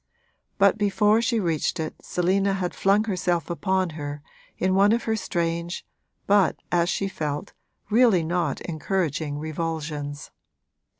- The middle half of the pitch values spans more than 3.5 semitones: Yes, average, 3.9 semitones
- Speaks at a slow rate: Yes, slow, 130 wpm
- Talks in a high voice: No, medium, 175 Hz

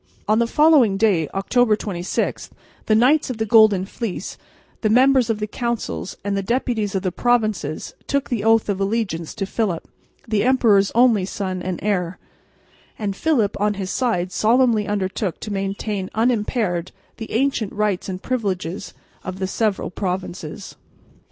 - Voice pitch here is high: Yes, high, 210 Hz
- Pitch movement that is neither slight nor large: Yes, average, 3.4 semitones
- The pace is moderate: Yes, average, 155 wpm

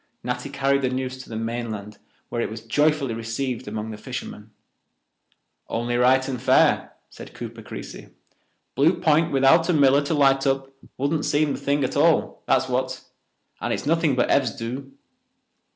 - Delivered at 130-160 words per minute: No, average, 170 wpm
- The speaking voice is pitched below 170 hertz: Yes, low, 135 Hz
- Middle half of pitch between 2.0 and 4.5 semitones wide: Yes, average, 3.3 semitones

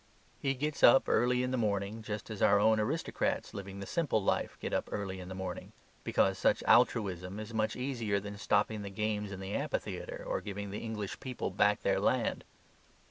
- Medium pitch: No, low, 105 Hz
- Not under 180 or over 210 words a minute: Yes, average, 195 wpm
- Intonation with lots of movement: No, narrow, 2.6 semitones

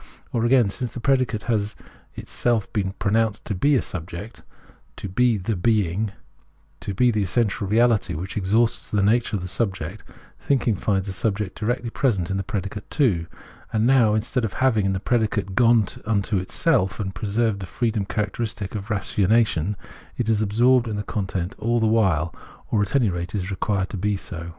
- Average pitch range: Yes, average, 3.2 semitones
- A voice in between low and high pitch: No, low, 105 Hz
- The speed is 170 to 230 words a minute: Yes, average, 185 wpm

